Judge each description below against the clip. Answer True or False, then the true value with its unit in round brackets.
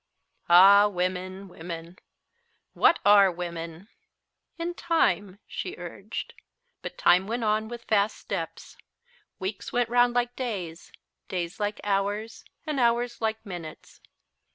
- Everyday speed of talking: False (120 wpm)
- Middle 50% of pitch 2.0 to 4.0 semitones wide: False (4.5 semitones)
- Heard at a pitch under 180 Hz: False (205 Hz)